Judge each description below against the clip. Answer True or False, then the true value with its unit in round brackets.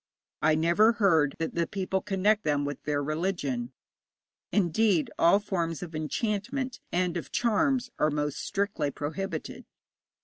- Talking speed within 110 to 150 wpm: True (135 wpm)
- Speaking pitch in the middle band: True (175 Hz)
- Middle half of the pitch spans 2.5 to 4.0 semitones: False (5.1 semitones)